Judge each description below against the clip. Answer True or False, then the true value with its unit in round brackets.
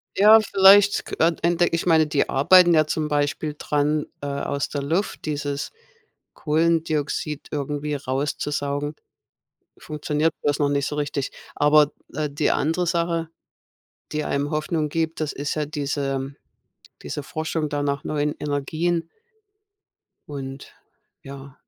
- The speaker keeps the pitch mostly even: True (2.1 semitones)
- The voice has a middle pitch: True (150 Hz)